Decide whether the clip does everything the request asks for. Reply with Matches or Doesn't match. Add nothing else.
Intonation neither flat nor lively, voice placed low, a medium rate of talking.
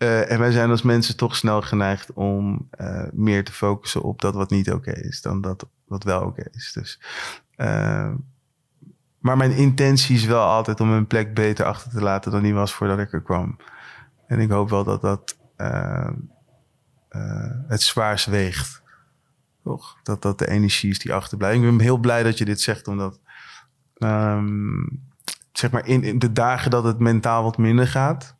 Matches